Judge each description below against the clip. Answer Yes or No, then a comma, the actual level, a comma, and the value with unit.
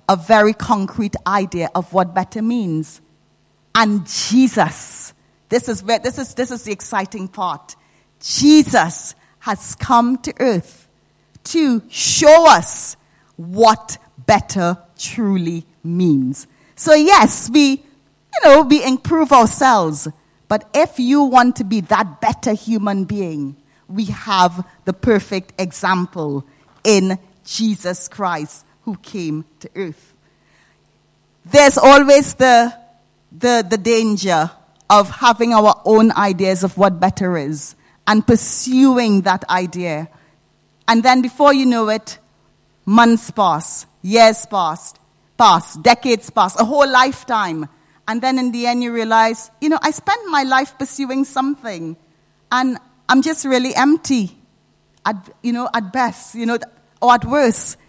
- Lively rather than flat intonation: Yes, wide, 5.7 semitones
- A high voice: Yes, high, 220 Hz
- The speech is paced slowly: Yes, slow, 130 wpm